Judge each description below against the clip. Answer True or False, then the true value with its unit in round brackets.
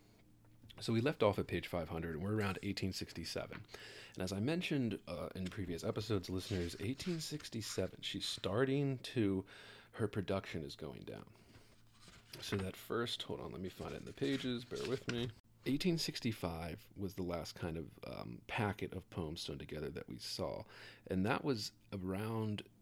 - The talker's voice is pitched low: True (105 Hz)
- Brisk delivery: False (165 wpm)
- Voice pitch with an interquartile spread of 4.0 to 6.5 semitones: False (3.6 semitones)